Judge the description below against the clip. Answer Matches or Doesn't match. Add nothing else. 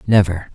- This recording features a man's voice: Matches